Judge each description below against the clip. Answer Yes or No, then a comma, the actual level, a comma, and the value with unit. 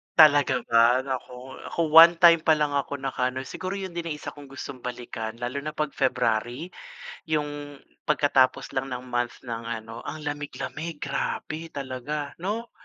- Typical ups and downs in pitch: Yes, average, 3.3 semitones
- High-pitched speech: No, medium, 140 Hz